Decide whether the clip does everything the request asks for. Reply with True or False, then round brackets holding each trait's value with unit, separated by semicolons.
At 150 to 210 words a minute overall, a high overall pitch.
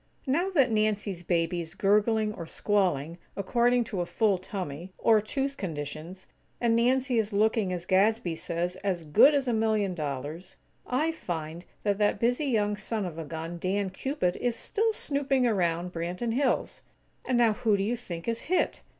True (175 wpm; 205 Hz)